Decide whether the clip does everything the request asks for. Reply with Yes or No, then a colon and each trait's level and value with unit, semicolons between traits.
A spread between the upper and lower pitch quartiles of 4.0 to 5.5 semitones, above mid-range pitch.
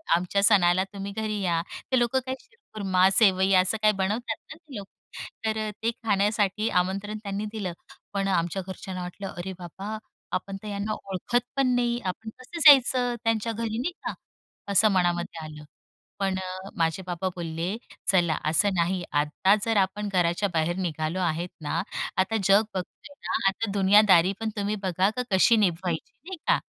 No: average, 3.4 semitones; high, 195 Hz